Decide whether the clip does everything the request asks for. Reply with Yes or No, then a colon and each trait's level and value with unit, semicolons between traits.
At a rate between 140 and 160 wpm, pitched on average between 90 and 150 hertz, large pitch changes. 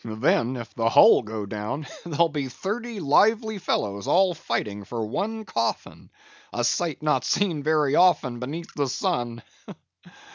Yes: average, 145 wpm; medium, 140 Hz; wide, 7.0 semitones